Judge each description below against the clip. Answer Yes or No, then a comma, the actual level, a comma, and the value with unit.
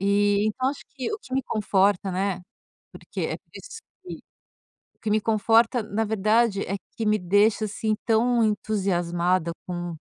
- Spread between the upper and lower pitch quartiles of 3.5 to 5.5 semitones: No, average, 2.7 semitones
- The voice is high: Yes, high, 210 Hz